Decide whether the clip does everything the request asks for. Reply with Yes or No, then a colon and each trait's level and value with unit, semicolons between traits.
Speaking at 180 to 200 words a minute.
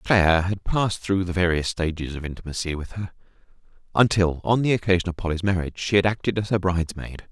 Yes: average, 195 wpm